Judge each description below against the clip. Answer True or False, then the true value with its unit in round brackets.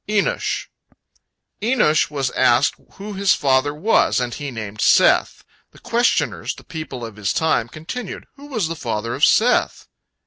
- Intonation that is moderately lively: False (9.0 semitones)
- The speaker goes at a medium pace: True (150 wpm)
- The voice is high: False (150 Hz)